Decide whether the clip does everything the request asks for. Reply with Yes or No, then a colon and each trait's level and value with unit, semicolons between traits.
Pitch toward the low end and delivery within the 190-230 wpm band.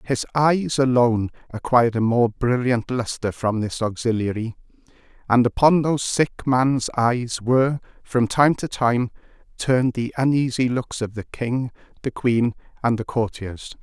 No: low, 120 Hz; average, 150 wpm